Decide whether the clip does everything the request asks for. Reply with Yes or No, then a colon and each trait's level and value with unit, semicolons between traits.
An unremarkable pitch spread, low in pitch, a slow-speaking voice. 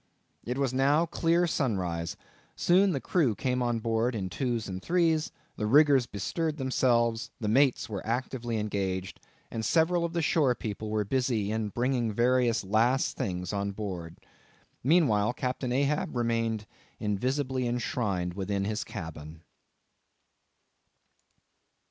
Yes: average, 4.5 semitones; low, 120 Hz; slow, 130 wpm